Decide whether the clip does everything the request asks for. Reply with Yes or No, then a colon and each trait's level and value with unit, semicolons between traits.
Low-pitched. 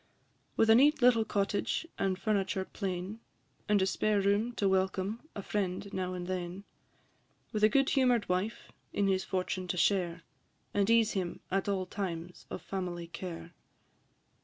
No: high, 195 Hz